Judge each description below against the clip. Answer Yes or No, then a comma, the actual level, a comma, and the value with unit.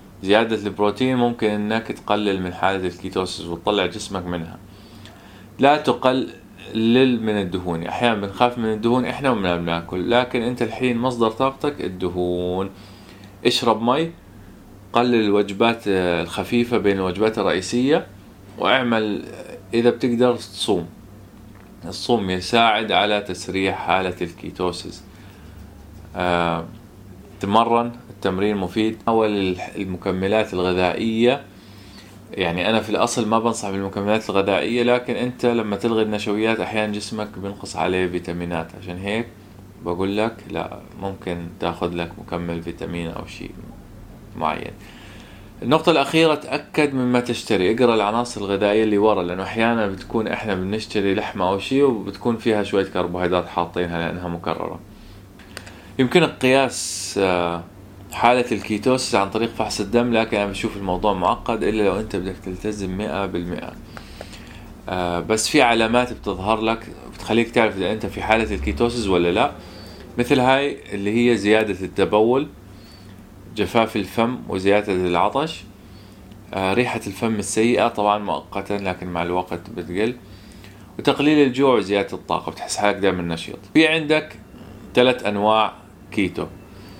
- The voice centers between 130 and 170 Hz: No, low, 105 Hz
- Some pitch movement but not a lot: Yes, average, 3.7 semitones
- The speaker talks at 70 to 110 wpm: No, average, 120 wpm